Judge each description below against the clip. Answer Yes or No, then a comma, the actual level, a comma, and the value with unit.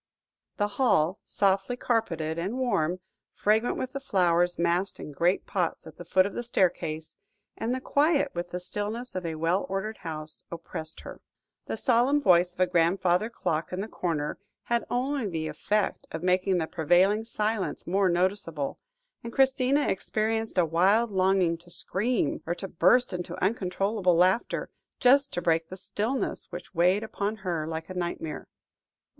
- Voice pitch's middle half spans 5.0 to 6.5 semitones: No, average, 4.3 semitones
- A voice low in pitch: No, medium, 185 Hz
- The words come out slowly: No, average, 160 wpm